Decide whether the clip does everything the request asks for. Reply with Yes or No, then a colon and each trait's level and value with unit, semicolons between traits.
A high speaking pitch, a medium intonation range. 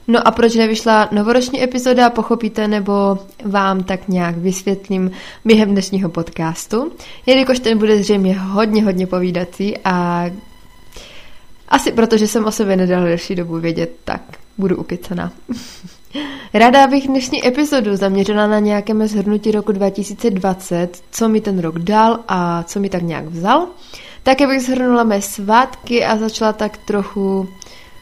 Yes: high, 210 Hz; average, 3.4 semitones